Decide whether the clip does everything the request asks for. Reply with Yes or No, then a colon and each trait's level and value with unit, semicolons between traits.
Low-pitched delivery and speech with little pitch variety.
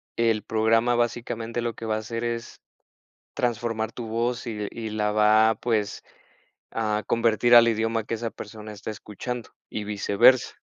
Yes: low, 115 Hz; narrow, 1.5 semitones